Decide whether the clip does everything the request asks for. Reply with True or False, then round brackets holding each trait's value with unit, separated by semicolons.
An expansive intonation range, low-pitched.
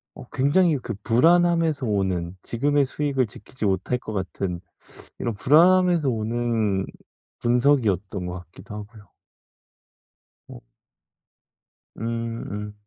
True (5.9 semitones; 120 Hz)